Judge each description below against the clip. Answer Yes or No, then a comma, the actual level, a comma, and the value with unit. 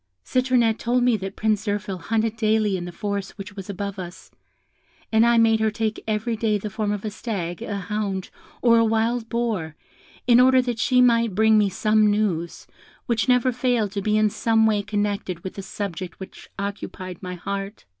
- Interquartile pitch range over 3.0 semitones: No, narrow, 2.5 semitones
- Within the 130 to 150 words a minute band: No, average, 195 wpm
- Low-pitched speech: No, high, 215 Hz